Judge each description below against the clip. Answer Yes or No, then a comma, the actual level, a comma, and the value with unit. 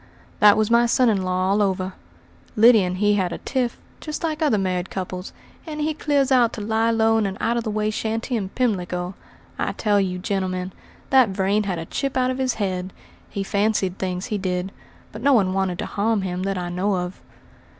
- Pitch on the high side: Yes, high, 205 Hz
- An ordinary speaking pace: No, fast, 215 wpm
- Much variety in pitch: No, average, 3.8 semitones